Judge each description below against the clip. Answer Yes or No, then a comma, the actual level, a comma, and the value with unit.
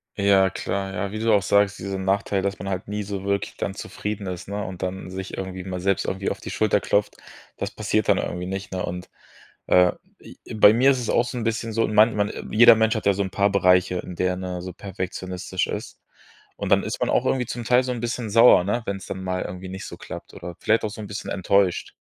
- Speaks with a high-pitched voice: No, low, 100 Hz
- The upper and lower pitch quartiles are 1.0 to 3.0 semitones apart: Yes, narrow, 2.4 semitones